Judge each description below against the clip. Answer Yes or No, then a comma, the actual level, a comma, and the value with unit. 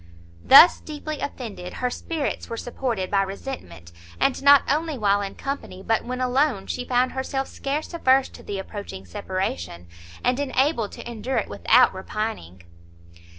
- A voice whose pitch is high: Yes, high, 245 Hz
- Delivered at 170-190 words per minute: No, average, 150 wpm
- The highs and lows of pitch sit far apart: Yes, wide, 5.7 semitones